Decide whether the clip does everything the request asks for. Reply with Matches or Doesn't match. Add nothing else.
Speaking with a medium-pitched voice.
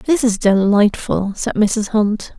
Doesn't match